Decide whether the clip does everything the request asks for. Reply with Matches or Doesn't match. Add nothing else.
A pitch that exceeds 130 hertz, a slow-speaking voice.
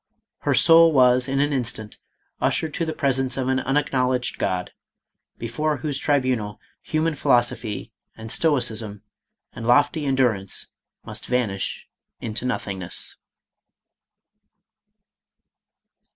Doesn't match